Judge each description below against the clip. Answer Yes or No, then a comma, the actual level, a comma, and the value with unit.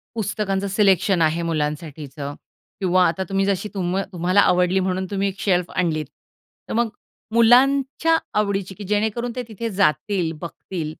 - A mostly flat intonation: No, average, 3.4 semitones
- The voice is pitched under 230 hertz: Yes, high, 190 Hz